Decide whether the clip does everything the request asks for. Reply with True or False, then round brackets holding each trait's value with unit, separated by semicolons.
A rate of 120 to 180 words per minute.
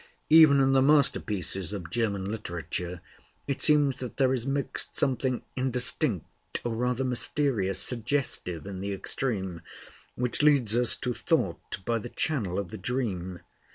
True (145 wpm)